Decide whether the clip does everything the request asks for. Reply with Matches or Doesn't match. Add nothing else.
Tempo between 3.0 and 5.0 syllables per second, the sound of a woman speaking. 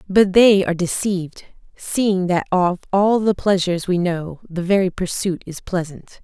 Matches